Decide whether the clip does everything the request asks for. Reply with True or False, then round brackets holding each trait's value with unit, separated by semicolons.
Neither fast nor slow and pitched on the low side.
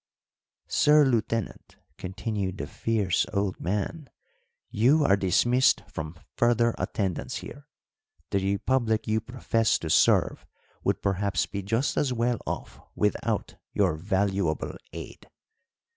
False (115 wpm; 105 Hz)